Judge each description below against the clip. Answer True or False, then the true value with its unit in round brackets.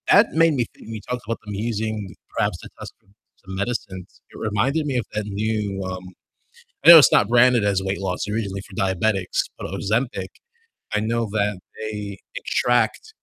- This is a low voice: True (105 Hz)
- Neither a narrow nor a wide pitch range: True (3.3 semitones)